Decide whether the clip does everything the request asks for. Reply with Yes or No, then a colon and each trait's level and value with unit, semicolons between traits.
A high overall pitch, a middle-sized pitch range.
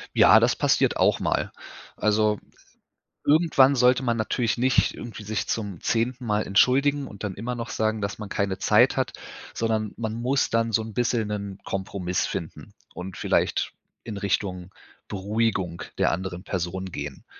No: low, 110 Hz; average, 3.2 semitones